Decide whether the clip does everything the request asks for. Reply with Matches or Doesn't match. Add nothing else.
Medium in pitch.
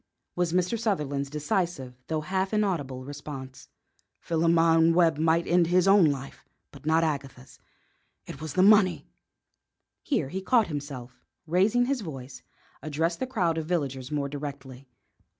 Matches